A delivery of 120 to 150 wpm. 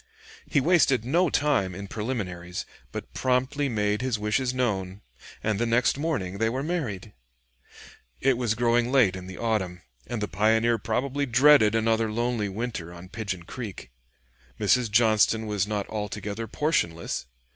Yes: average, 145 wpm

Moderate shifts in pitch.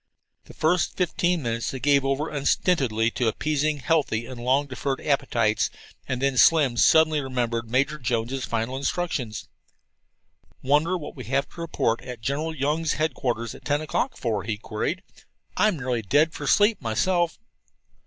Yes: average, 4.6 semitones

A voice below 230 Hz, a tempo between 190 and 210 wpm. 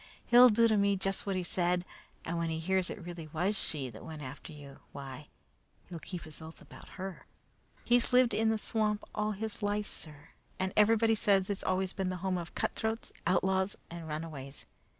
Yes: medium, 185 Hz; average, 195 wpm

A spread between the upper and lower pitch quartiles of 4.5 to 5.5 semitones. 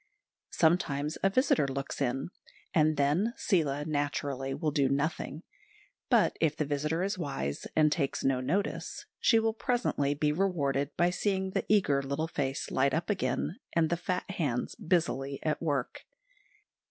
No: average, 4.1 semitones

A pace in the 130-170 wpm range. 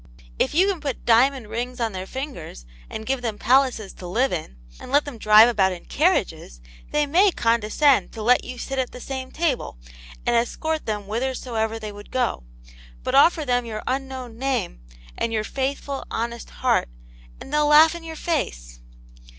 No: average, 185 wpm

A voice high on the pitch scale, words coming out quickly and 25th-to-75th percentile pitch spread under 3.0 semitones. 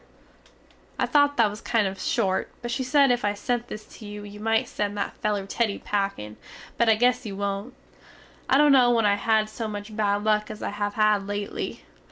Yes: high, 215 Hz; fast, 225 wpm; narrow, 2.6 semitones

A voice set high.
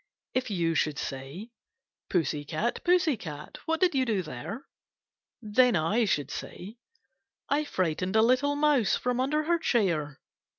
Yes: high, 220 Hz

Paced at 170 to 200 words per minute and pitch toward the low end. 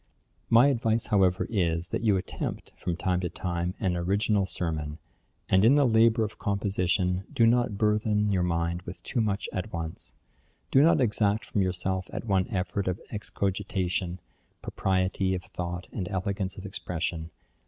No: average, 160 wpm; very low, 95 Hz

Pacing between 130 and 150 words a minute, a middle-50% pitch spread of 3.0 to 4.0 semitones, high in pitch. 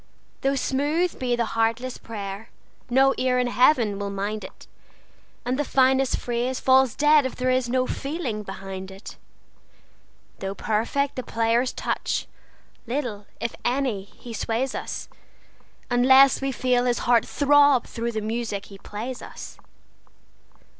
Yes: average, 140 wpm; average, 3.3 semitones; high, 245 Hz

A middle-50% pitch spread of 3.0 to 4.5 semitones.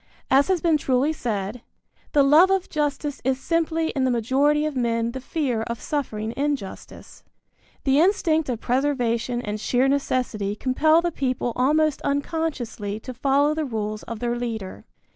Yes: average, 4.2 semitones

